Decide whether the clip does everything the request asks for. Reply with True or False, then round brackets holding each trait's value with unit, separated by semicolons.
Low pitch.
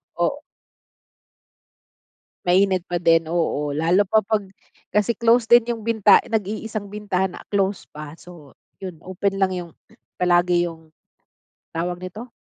False (185 Hz)